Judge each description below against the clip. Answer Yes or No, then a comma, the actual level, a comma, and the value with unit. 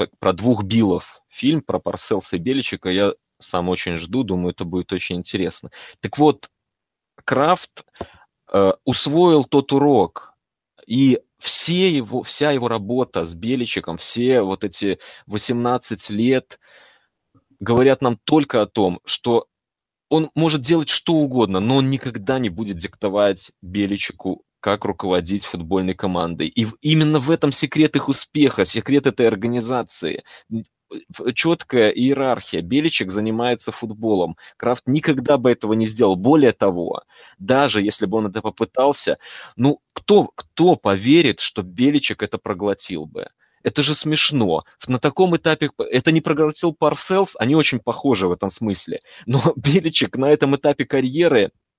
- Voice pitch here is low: Yes, low, 125 Hz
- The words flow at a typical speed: Yes, average, 140 wpm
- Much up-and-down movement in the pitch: Yes, wide, 6.0 semitones